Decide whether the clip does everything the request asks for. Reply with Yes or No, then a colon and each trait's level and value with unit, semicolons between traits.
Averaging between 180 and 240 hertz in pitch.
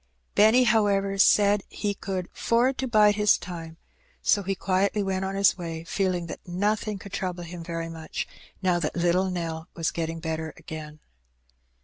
Yes: medium, 185 Hz